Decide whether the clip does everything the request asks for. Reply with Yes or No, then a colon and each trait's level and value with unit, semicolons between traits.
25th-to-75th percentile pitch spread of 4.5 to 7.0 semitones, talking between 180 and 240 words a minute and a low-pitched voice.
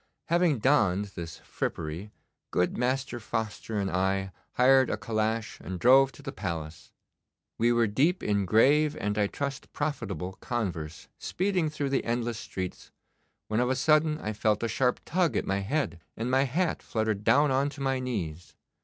No: wide, 5.6 semitones; average, 170 wpm; low, 115 Hz